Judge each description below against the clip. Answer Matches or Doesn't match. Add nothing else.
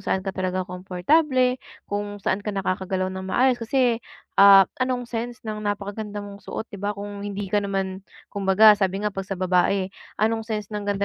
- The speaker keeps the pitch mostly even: Matches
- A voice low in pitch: Doesn't match